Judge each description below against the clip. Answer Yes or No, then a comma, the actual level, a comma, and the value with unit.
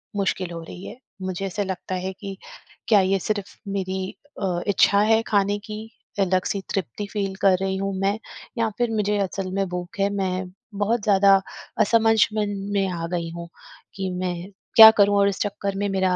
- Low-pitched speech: No, high, 195 Hz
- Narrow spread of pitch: Yes, narrow, 1.6 semitones